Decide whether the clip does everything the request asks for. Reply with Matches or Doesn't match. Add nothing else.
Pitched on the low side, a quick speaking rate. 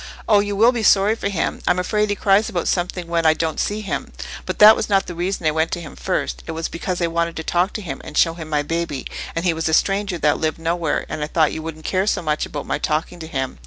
Doesn't match